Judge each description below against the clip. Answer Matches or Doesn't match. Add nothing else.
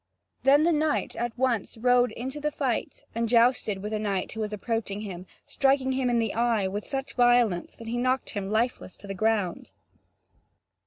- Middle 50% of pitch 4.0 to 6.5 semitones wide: Doesn't match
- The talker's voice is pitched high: Matches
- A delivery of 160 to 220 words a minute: Matches